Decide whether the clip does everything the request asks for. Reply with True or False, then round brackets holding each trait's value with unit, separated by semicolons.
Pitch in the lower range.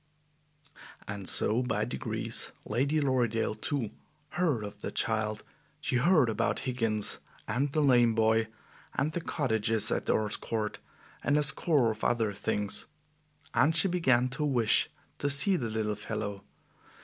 True (120 Hz)